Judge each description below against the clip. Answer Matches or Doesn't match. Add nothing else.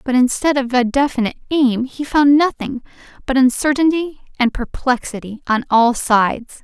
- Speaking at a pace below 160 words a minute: Matches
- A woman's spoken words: Matches